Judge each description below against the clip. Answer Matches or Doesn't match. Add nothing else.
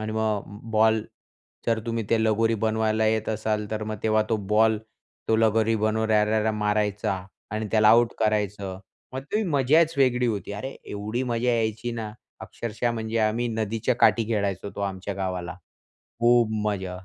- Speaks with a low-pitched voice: Matches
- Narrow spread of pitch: Matches